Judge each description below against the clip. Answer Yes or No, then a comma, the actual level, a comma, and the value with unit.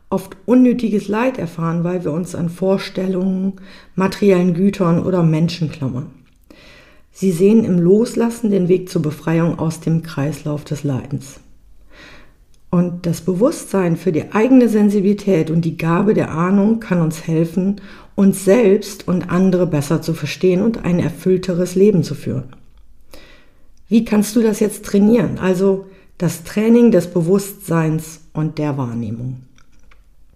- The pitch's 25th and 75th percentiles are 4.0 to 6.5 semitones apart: No, average, 3.6 semitones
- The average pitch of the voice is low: No, medium, 180 Hz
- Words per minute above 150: No, average, 135 wpm